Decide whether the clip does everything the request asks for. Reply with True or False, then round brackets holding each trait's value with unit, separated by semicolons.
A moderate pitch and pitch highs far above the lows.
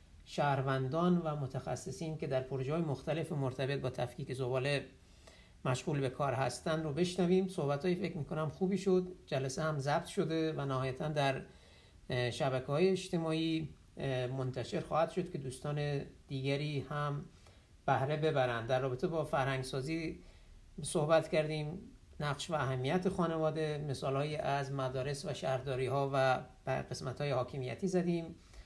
False (145 Hz; 3.6 semitones)